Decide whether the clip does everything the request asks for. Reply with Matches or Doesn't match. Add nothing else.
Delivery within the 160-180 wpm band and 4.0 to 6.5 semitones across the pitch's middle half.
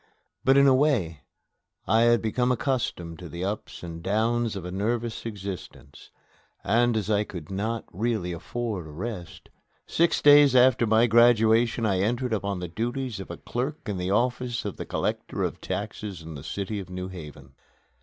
Matches